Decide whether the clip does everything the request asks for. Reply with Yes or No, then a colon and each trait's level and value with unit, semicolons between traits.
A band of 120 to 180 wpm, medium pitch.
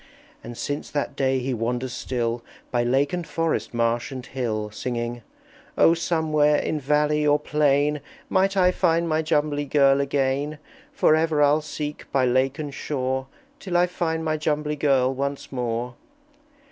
Yes: average, 160 wpm; medium, 145 Hz